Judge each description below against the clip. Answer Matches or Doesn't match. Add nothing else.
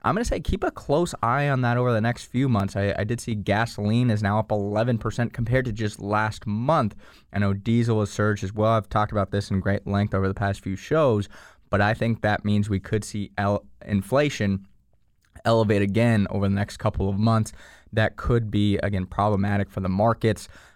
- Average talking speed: Doesn't match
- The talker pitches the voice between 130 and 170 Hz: Doesn't match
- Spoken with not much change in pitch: Matches